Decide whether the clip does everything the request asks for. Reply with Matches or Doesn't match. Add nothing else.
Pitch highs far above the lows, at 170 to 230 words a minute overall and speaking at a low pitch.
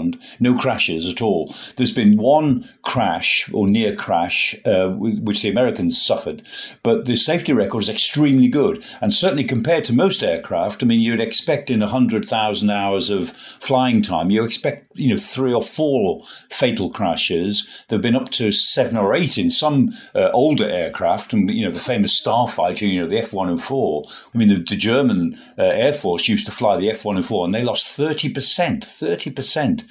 Matches